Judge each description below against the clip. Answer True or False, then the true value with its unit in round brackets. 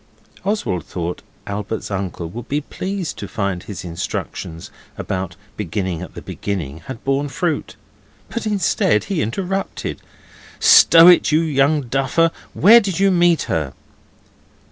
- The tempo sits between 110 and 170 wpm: True (135 wpm)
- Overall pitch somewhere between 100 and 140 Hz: True (135 Hz)